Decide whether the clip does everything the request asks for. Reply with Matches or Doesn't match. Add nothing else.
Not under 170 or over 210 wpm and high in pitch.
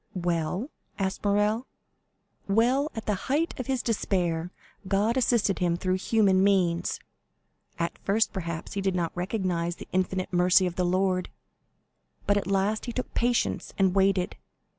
Doesn't match